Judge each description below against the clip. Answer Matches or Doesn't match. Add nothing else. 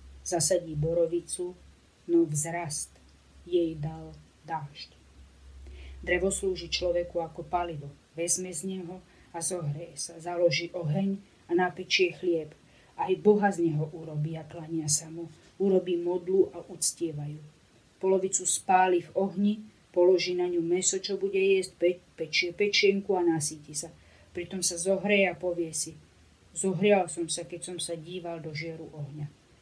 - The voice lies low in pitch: Doesn't match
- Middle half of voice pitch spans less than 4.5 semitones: Matches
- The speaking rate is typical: Matches